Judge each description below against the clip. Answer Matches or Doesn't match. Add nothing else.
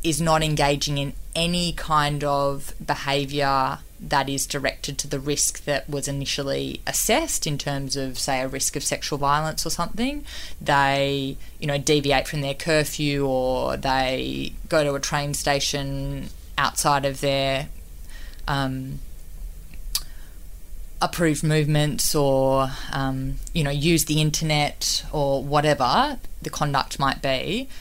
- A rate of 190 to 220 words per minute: Doesn't match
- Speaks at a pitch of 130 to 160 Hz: Matches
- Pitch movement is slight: Matches